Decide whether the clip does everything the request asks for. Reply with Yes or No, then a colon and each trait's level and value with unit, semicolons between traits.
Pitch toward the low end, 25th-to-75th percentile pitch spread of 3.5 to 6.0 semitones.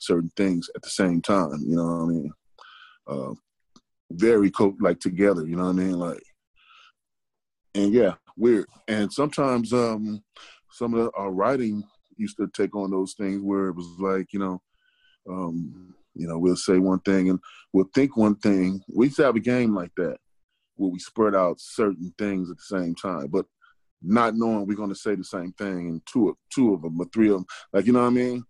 No: very low, 95 Hz; average, 2.9 semitones